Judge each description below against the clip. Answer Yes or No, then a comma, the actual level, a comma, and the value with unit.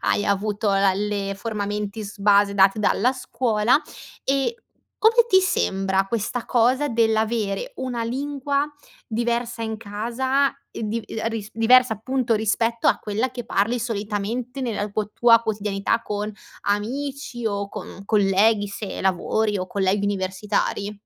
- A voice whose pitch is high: Yes, high, 220 Hz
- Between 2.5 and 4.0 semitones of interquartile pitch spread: Yes, average, 2.9 semitones